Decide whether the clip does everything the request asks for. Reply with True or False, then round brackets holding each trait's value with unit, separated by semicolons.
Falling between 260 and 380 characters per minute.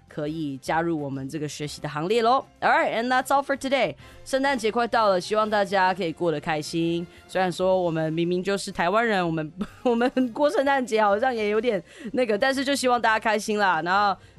False (400 characters per minute)